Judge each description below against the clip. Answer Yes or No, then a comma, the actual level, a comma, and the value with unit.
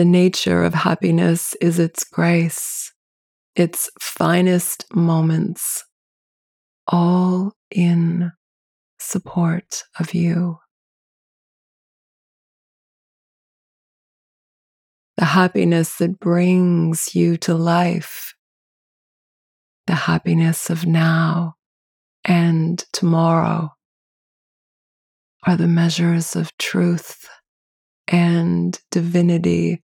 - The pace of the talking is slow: Yes, slow, 70 wpm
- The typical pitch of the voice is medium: Yes, medium, 170 Hz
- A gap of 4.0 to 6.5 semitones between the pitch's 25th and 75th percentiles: No, narrow, 1.2 semitones